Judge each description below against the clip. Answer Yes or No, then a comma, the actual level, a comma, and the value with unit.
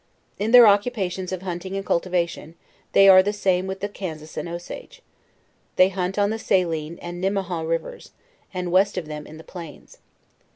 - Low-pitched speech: No, medium, 185 Hz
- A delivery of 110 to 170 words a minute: No, average, 180 wpm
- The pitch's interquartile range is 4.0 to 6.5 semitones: No, narrow, 2.4 semitones